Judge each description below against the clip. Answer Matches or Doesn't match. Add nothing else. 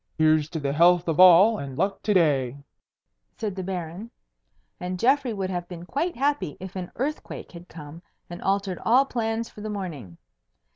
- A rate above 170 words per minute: Matches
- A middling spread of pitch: Matches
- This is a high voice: Doesn't match